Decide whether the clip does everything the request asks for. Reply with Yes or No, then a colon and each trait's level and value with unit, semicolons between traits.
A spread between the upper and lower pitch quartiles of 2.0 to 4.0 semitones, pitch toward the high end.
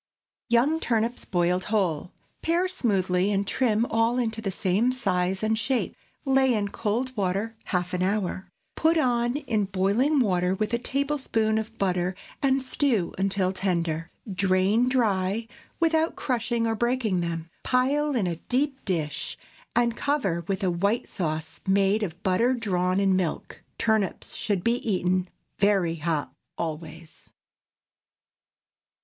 No: average, 4.8 semitones; high, 205 Hz